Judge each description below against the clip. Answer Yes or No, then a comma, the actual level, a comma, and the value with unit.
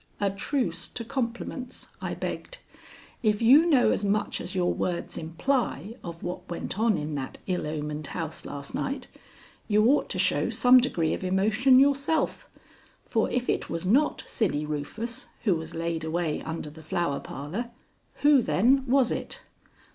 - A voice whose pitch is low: No, high, 195 Hz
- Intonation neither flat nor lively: No, wide, 7.4 semitones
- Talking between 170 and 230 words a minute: No, average, 160 wpm